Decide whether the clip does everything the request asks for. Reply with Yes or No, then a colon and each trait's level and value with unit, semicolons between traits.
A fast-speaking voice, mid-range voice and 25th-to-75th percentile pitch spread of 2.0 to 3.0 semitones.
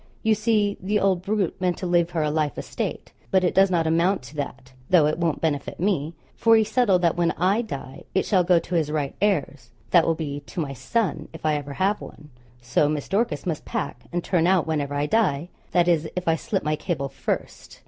No: fast, 230 wpm; medium, 170 Hz; average, 4.2 semitones